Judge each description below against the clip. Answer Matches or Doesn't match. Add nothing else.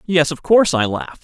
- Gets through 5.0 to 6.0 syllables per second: Doesn't match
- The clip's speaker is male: Matches